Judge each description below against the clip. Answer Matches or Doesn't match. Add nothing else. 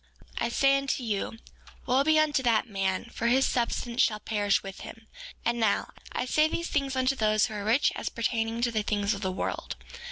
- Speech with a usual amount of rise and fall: Matches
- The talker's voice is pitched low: Doesn't match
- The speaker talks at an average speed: Doesn't match